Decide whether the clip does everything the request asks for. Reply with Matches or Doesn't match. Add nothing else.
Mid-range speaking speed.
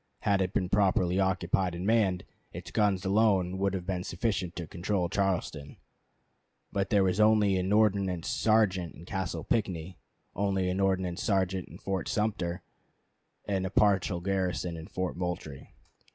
Matches